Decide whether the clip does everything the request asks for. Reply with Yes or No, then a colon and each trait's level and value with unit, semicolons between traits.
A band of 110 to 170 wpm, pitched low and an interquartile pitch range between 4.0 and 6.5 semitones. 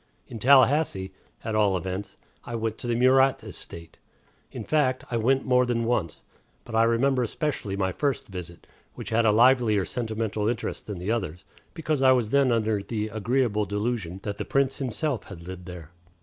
No: average, 180 wpm; low, 115 Hz; average, 4.3 semitones